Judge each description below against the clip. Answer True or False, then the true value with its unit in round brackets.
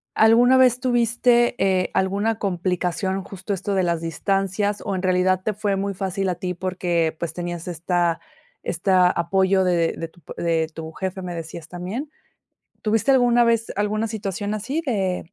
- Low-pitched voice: False (190 Hz)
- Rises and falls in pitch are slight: False (3.3 semitones)